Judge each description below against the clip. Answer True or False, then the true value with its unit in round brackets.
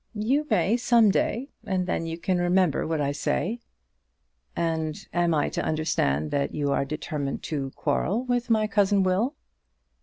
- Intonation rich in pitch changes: True (5.9 semitones)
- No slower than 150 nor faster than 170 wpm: True (160 wpm)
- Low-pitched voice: False (175 Hz)